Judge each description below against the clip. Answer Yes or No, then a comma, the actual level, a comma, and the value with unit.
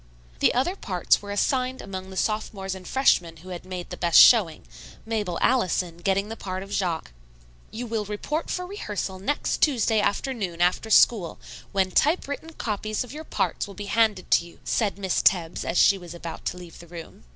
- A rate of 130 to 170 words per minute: No, average, 185 wpm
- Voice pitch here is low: No, high, 200 Hz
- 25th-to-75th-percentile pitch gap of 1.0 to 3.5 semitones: No, average, 4.0 semitones